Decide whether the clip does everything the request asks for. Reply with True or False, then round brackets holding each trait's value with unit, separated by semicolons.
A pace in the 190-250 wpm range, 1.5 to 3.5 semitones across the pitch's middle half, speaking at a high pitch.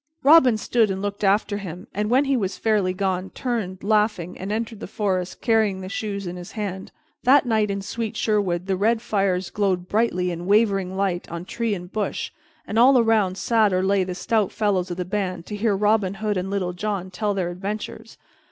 True (205 wpm; 2.8 semitones; 200 Hz)